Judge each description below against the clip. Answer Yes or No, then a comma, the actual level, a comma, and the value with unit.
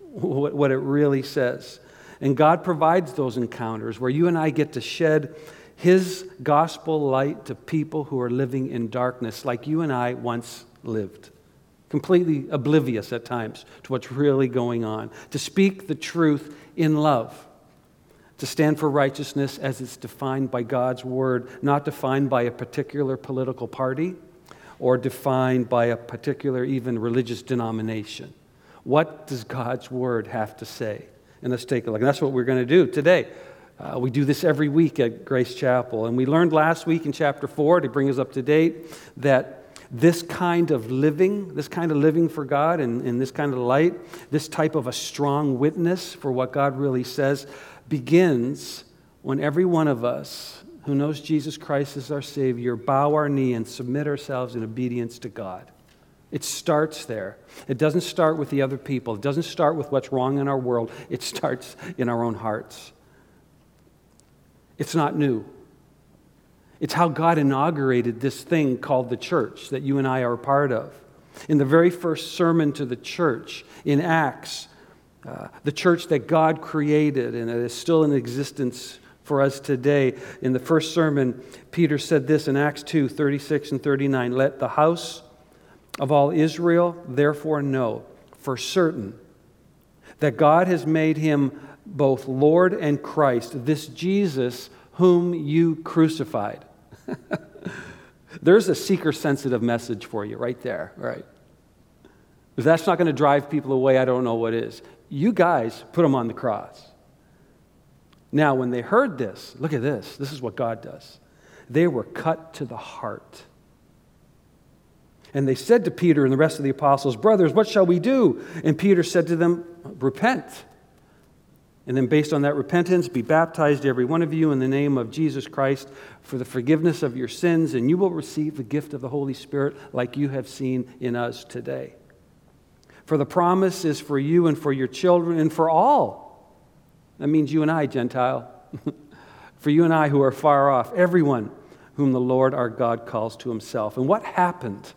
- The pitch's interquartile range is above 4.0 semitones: No, average, 3.6 semitones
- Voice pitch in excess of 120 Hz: Yes, medium, 140 Hz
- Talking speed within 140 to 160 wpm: No, average, 175 wpm